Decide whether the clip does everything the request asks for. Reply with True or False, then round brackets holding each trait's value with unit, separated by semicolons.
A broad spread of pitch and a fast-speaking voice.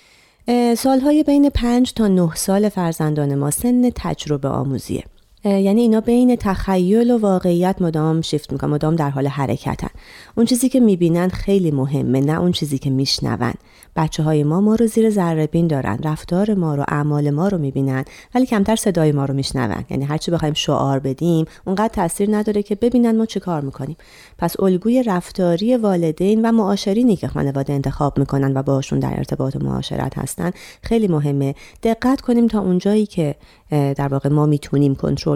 True (6.9 semitones; 170 wpm)